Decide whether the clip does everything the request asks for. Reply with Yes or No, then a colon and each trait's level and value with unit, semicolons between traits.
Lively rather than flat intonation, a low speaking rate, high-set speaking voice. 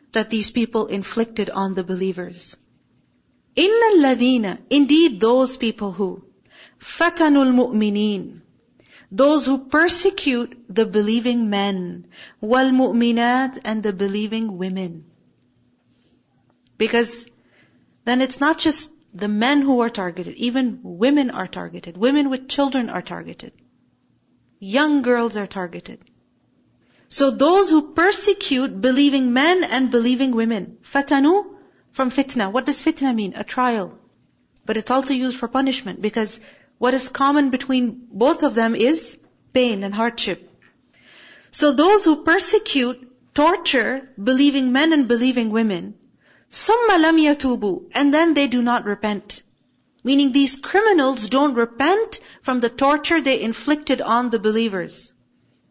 No: average, 4.4 semitones; slow, 125 wpm; very high, 255 Hz